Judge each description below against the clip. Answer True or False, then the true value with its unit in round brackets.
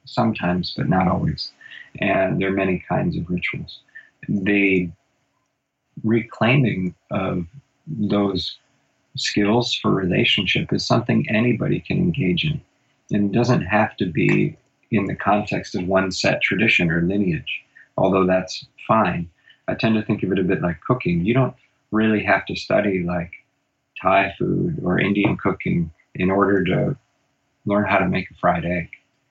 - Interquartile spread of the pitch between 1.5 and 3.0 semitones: False (4.3 semitones)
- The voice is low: True (100 Hz)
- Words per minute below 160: True (150 wpm)